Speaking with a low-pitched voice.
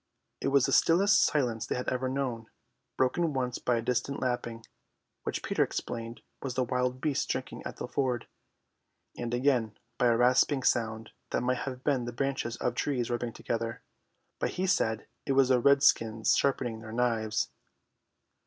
Yes: low, 125 Hz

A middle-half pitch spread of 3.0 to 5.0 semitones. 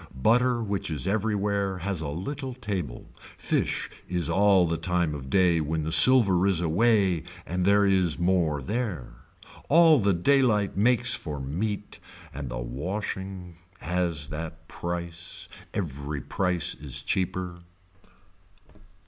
Yes: average, 4.2 semitones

